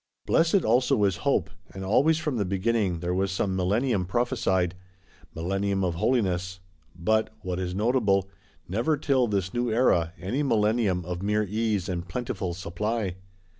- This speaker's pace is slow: No, average, 150 wpm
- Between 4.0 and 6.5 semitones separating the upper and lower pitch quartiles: Yes, average, 4.3 semitones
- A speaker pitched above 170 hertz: No, low, 100 Hz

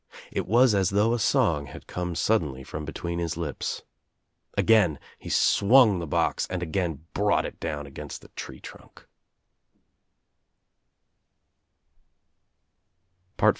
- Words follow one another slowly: Yes, slow, 125 wpm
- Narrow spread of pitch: No, average, 4.9 semitones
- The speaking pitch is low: Yes, very low, 85 Hz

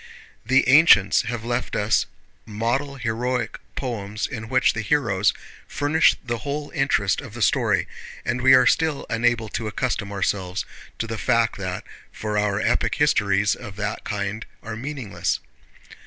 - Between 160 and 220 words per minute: No, average, 150 wpm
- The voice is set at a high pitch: No, low, 115 Hz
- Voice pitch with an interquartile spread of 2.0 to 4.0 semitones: Yes, average, 3.6 semitones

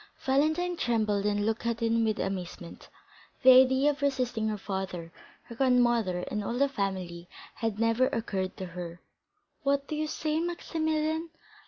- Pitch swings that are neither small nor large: No, wide, 5.9 semitones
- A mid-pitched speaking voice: No, high, 230 Hz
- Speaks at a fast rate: No, average, 155 wpm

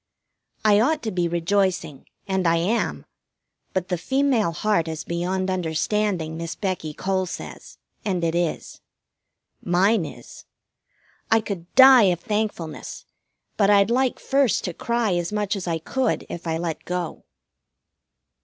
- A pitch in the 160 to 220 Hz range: Yes, medium, 185 Hz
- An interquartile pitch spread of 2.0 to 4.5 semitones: Yes, average, 3.9 semitones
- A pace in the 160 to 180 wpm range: No, average, 145 wpm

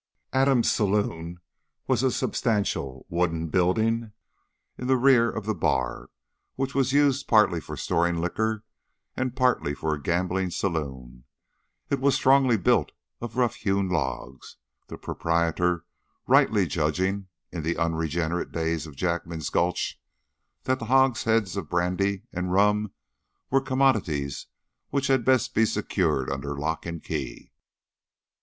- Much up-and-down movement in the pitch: Yes, wide, 6.5 semitones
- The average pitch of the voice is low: Yes, very low, 95 Hz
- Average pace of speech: No, slow, 130 wpm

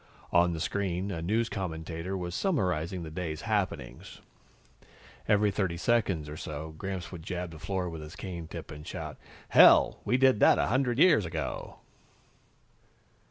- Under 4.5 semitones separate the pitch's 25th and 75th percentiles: Yes, average, 3.9 semitones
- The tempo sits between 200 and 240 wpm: No, average, 160 wpm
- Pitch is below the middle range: Yes, very low, 90 Hz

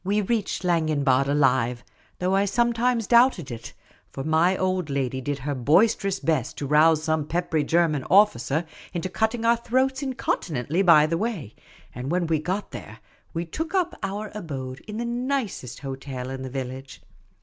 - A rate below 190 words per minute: Yes, average, 170 wpm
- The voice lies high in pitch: No, medium, 165 Hz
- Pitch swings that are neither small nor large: No, wide, 7.4 semitones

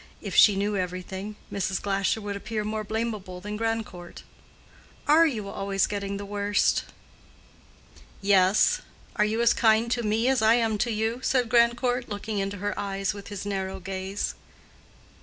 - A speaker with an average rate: Yes, average, 160 wpm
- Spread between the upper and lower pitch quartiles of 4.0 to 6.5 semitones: No, narrow, 2.4 semitones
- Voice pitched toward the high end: Yes, high, 205 Hz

